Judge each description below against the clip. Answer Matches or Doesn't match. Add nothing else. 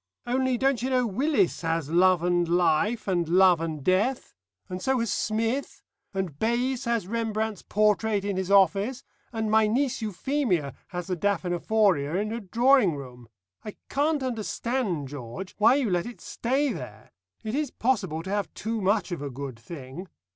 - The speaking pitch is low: Doesn't match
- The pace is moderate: Matches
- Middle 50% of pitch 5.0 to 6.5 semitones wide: Matches